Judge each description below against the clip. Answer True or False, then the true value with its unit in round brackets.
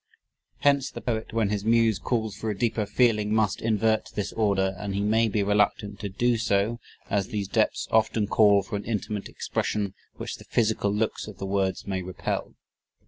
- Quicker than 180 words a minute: True (190 wpm)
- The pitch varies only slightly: True (1.9 semitones)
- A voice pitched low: True (105 Hz)